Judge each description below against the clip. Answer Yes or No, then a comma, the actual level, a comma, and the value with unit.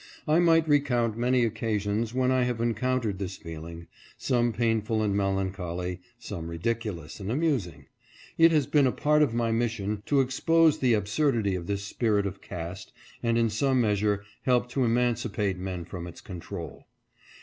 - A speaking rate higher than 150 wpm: Yes, average, 170 wpm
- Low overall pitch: Yes, low, 115 Hz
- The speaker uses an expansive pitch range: No, average, 4.4 semitones